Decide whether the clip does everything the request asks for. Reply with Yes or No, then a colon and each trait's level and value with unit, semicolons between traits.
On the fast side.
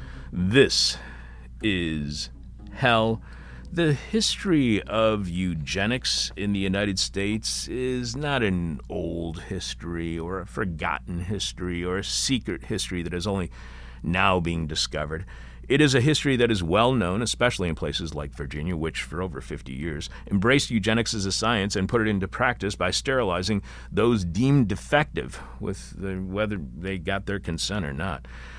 No: average, 150 wpm